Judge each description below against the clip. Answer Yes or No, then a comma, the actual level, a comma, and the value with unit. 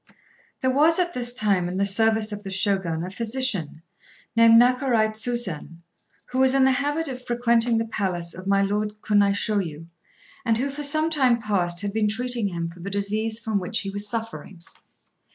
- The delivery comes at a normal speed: Yes, average, 190 wpm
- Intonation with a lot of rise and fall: No, average, 3.8 semitones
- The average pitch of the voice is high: Yes, high, 220 Hz